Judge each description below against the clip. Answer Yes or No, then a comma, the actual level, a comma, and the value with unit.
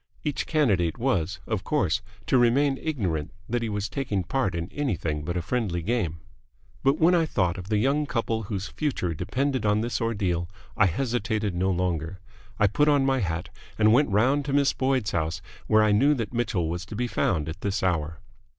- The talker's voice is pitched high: No, low, 105 Hz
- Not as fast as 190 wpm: No, average, 195 wpm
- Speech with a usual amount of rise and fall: No, wide, 6.8 semitones